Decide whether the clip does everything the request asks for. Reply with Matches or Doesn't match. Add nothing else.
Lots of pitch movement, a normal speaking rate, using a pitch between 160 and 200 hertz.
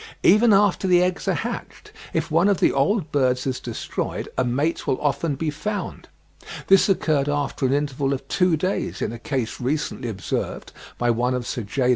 Doesn't match